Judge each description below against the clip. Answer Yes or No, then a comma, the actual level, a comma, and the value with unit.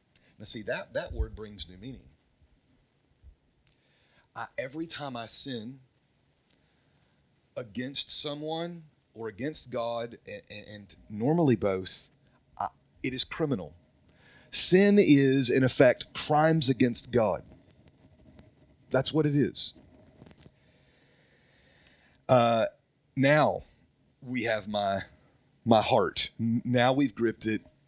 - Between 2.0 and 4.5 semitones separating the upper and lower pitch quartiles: No, average, 4.9 semitones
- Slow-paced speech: Yes, slow, 105 wpm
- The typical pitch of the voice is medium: No, low, 125 Hz